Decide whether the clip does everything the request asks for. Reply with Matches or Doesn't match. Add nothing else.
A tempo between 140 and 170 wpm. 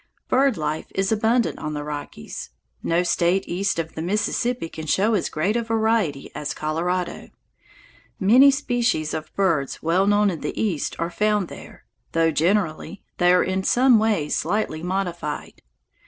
Matches